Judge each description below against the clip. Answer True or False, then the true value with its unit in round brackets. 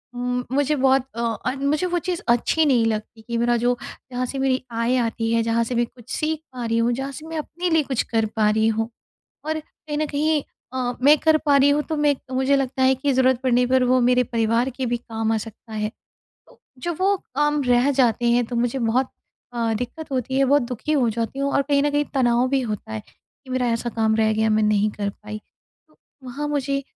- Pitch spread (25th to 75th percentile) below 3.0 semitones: False (3.4 semitones)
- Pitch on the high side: True (255 Hz)